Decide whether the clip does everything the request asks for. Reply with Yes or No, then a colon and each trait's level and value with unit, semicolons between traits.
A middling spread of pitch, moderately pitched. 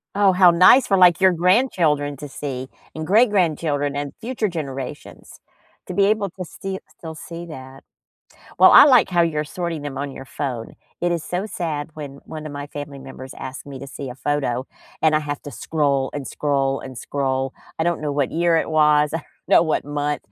Yes: average, 3.7 semitones; medium, 150 Hz